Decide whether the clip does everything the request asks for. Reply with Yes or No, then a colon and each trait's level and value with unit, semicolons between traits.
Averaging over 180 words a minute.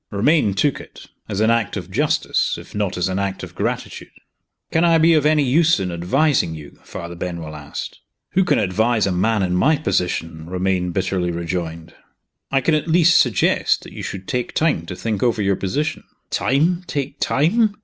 Yes: average, 190 wpm